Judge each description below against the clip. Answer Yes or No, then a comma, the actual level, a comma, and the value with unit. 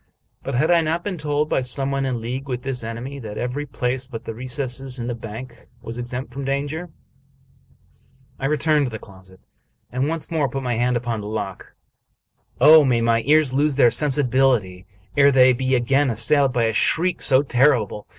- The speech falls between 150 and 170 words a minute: No, average, 190 wpm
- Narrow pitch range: No, average, 3.1 semitones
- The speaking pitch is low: Yes, low, 130 Hz